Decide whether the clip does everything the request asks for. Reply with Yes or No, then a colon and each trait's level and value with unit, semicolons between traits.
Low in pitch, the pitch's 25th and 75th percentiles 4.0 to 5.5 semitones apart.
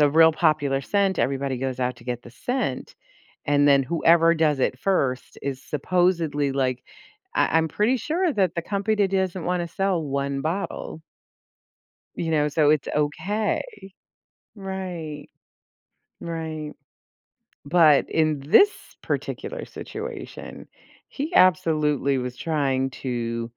No: medium, 155 Hz; average, 4.9 semitones